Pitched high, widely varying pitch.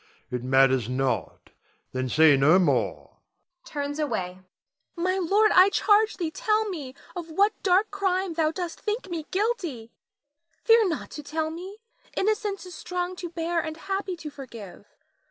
Yes: very high, 335 Hz; wide, 8.0 semitones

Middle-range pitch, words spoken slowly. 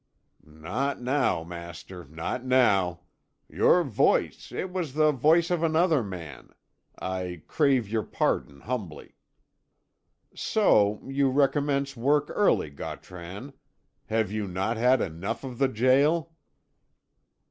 No: low, 125 Hz; slow, 115 wpm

